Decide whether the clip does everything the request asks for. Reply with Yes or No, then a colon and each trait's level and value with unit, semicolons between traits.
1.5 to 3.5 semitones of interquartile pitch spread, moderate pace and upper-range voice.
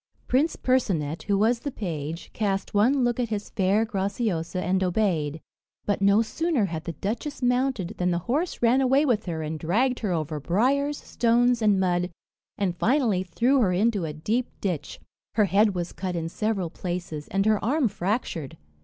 No: wide, 5.4 semitones; average, 180 wpm; high, 200 Hz